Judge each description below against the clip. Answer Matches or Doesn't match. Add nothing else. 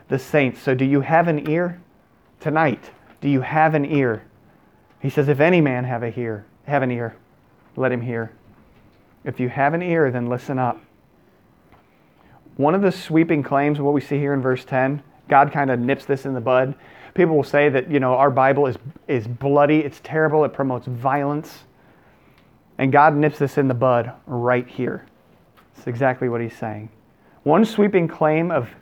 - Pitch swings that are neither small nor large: Matches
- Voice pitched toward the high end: Doesn't match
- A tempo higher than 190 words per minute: Doesn't match